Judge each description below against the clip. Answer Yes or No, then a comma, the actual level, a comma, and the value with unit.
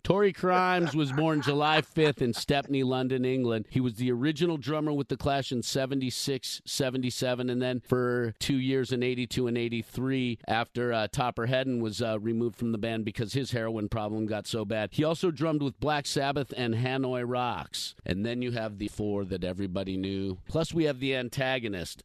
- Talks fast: No, average, 195 wpm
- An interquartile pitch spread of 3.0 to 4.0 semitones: Yes, average, 3.5 semitones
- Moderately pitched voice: No, low, 125 Hz